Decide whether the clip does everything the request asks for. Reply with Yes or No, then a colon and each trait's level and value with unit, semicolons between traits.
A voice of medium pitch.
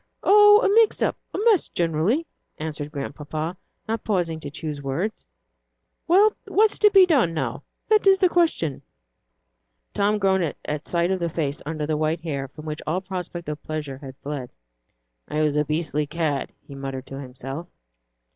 Yes: medium, 160 Hz